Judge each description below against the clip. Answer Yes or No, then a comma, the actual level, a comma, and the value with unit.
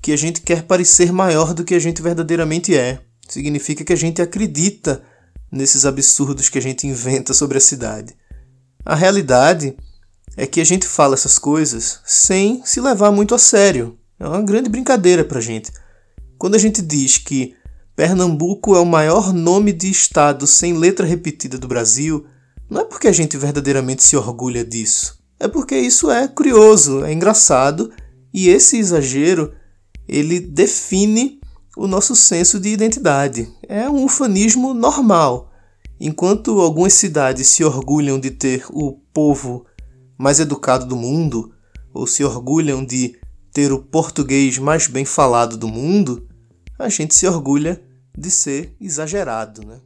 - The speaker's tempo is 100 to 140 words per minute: No, average, 155 wpm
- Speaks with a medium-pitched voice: Yes, medium, 145 Hz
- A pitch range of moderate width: No, wide, 6.3 semitones